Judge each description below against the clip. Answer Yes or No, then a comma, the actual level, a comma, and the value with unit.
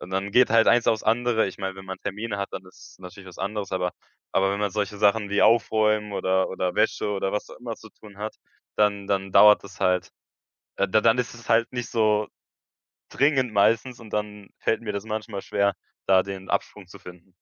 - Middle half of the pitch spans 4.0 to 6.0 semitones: No, narrow, 2.4 semitones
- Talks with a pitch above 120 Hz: No, low, 105 Hz